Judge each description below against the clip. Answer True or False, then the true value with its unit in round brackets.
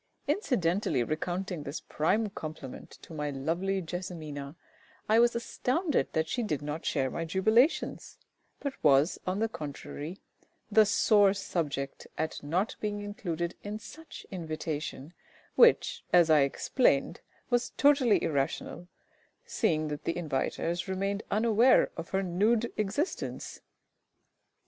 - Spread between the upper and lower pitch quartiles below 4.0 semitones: False (5.6 semitones)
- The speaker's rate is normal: False (125 wpm)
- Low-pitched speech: False (180 Hz)